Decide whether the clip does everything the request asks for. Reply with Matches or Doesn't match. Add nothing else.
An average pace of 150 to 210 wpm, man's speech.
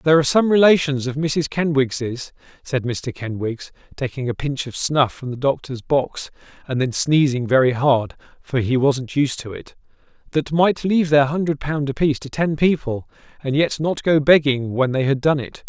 Matches